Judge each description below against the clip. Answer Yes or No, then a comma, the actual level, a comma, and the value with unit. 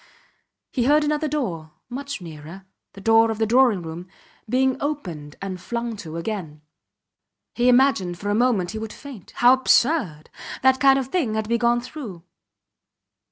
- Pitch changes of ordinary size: No, wide, 6.5 semitones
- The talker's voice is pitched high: Yes, high, 225 Hz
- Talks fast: No, average, 165 wpm